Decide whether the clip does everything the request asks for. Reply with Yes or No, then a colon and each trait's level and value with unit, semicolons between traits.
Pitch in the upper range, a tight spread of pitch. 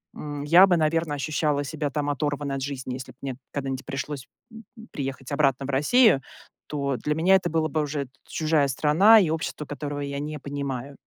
No: medium, 145 Hz; narrow, 2.1 semitones